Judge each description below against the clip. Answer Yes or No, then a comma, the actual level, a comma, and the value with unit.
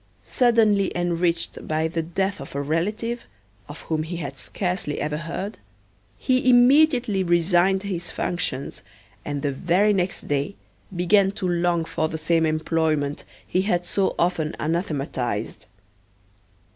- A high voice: No, medium, 175 Hz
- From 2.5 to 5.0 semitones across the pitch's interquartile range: Yes, average, 3.7 semitones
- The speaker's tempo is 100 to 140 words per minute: Yes, slow, 135 wpm